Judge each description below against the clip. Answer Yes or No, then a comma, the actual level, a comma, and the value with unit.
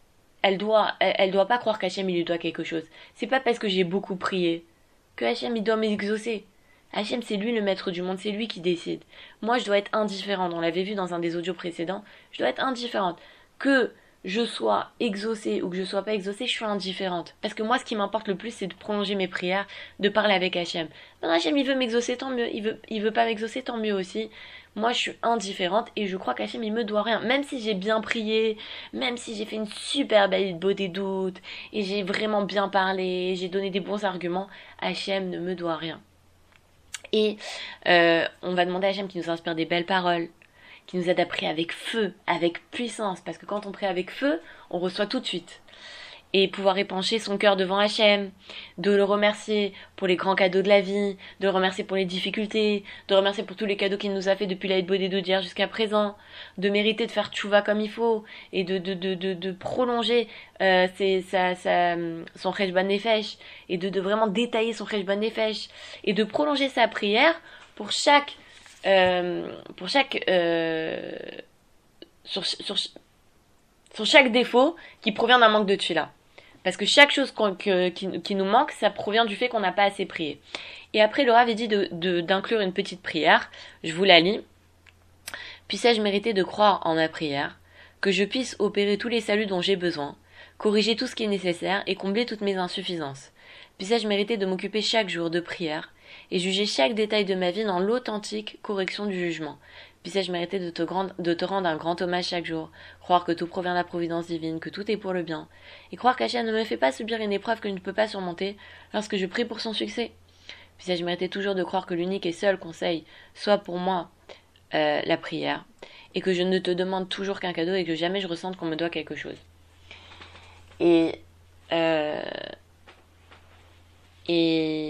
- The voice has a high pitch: Yes, high, 195 Hz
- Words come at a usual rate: Yes, average, 210 wpm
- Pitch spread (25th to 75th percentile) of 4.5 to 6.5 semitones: No, average, 3.5 semitones